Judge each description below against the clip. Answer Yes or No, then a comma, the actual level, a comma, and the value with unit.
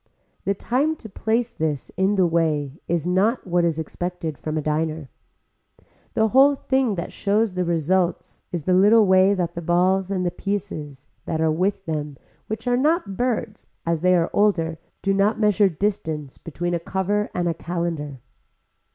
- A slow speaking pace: No, average, 175 wpm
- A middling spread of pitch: Yes, average, 4.1 semitones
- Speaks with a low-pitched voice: No, medium, 180 Hz